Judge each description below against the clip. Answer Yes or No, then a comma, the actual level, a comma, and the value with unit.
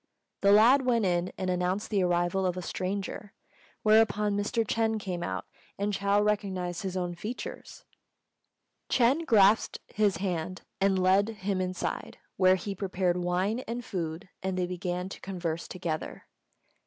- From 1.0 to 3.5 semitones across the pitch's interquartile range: Yes, narrow, 2.5 semitones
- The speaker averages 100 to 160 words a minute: Yes, average, 150 wpm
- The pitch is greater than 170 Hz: Yes, high, 190 Hz